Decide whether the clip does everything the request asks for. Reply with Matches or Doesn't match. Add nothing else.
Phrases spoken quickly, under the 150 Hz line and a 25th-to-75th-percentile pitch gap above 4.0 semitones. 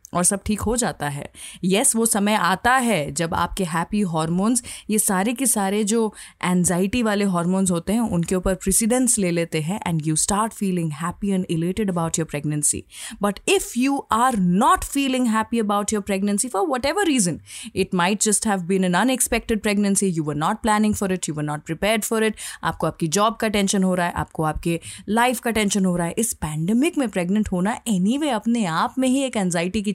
Doesn't match